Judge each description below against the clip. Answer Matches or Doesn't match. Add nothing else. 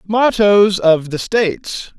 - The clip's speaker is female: Doesn't match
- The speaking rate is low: Matches